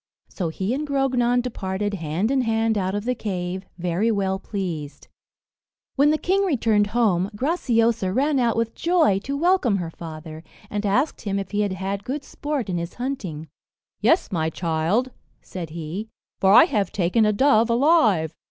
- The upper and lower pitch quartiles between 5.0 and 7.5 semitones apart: Yes, wide, 5.5 semitones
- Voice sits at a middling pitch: No, high, 210 Hz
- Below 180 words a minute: Yes, average, 170 wpm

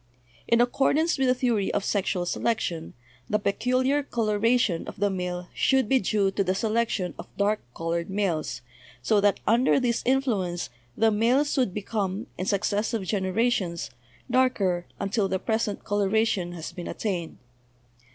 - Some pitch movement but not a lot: Yes, average, 4.0 semitones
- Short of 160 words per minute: Yes, average, 150 wpm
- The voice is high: Yes, high, 205 Hz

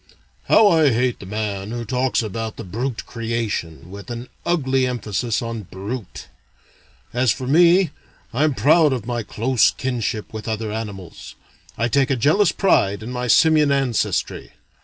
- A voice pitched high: No, low, 120 Hz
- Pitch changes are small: No, average, 3.6 semitones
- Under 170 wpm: Yes, average, 160 wpm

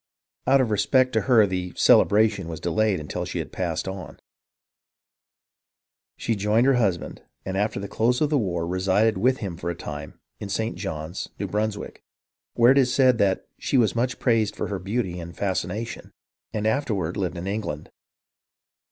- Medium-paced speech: Yes, average, 170 wpm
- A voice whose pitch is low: Yes, low, 105 Hz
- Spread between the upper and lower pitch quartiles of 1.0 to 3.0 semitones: No, average, 4.1 semitones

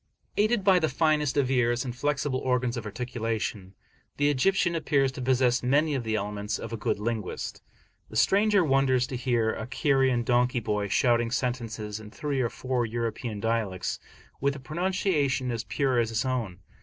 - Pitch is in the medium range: No, low, 125 Hz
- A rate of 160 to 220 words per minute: Yes, average, 175 wpm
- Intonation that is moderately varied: Yes, average, 3.5 semitones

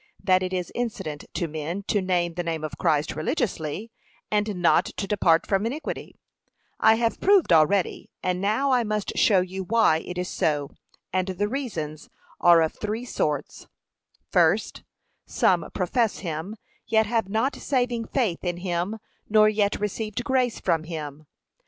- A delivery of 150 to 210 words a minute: Yes, average, 160 wpm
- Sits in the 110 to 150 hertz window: No, high, 190 Hz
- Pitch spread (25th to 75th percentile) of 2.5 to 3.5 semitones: No, average, 4.8 semitones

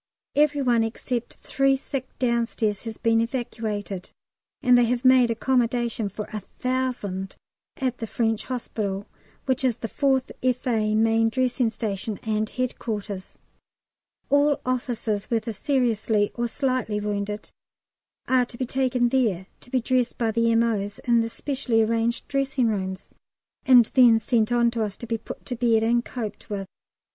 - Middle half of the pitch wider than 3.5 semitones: No, average, 2.7 semitones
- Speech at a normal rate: Yes, average, 150 wpm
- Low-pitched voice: No, high, 235 Hz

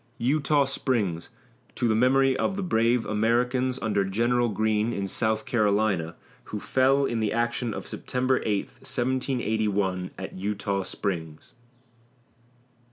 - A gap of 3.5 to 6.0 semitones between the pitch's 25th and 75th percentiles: Yes, average, 3.9 semitones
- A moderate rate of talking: No, slow, 125 wpm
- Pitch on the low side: Yes, low, 110 Hz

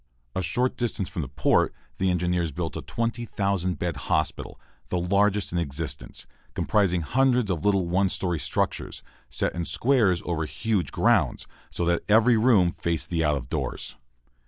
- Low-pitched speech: Yes, very low, 90 Hz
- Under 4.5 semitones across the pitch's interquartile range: Yes, average, 3.6 semitones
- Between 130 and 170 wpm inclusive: Yes, average, 160 wpm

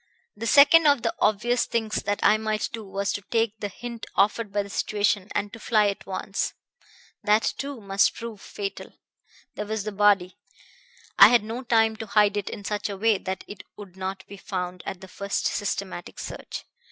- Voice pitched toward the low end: No, high, 205 Hz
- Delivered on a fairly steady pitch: Yes, narrow, 2.2 semitones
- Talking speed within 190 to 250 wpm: Yes, average, 195 wpm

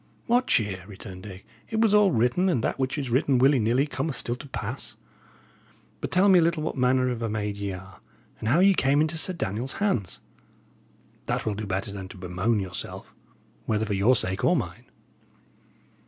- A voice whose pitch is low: Yes, low, 120 Hz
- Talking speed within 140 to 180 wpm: No, average, 200 wpm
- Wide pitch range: Yes, wide, 7.3 semitones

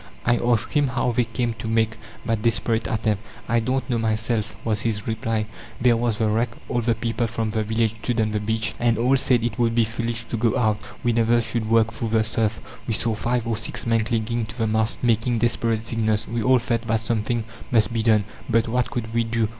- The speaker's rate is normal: No, fast, 230 wpm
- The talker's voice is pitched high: No, low, 115 Hz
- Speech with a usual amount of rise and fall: No, narrow, 1.1 semitones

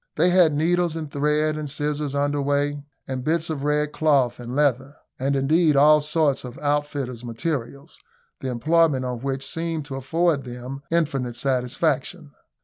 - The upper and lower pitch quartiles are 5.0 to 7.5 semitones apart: No, narrow, 2.5 semitones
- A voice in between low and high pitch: Yes, medium, 145 Hz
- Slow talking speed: No, average, 155 wpm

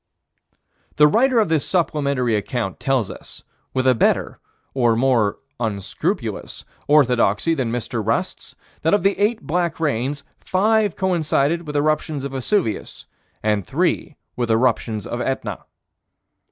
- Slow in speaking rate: Yes, slow, 130 wpm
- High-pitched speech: No, low, 135 Hz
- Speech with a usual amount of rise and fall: No, wide, 6.1 semitones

